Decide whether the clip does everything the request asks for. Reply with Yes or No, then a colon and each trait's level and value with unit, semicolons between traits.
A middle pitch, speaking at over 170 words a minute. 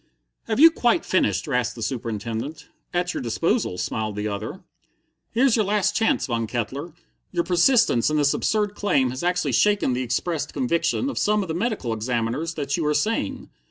Yes: medium, 150 Hz; average, 180 wpm